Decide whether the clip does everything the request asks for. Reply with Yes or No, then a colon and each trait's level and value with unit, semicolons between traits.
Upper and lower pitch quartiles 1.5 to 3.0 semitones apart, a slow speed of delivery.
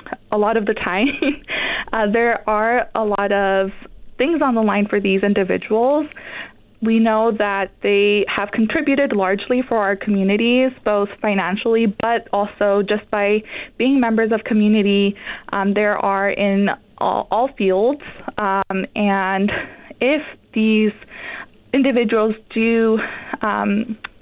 Yes: narrow, 2.6 semitones; slow, 130 wpm